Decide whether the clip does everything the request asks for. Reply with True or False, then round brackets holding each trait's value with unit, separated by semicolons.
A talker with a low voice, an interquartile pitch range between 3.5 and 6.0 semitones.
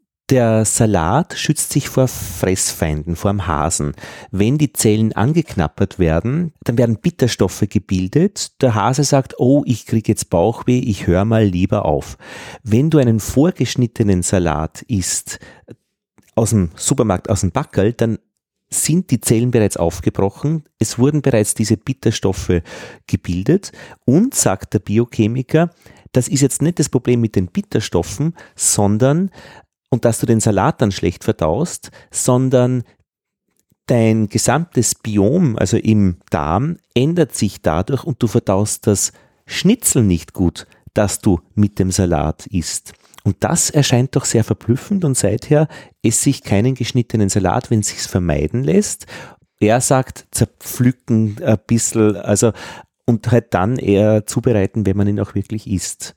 True (110 Hz; 4.6 semitones)